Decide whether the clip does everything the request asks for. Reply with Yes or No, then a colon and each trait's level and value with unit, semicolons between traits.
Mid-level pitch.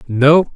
Yes: medium, 145 Hz